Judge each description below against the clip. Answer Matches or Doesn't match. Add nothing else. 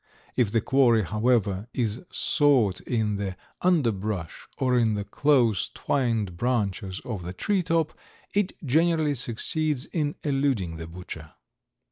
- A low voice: Matches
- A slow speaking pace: Matches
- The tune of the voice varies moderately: Doesn't match